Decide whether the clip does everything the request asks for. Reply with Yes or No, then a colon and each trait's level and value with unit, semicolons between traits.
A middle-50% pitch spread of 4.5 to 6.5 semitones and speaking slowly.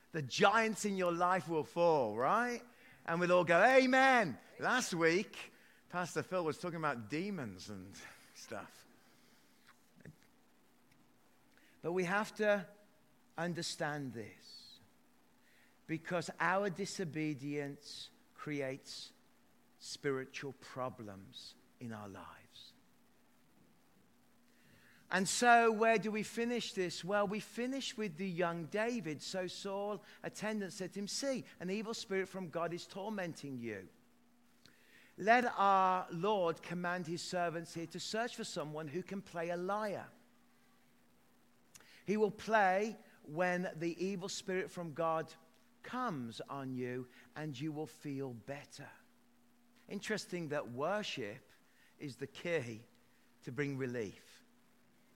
Yes: wide, 5.4 semitones; slow, 120 wpm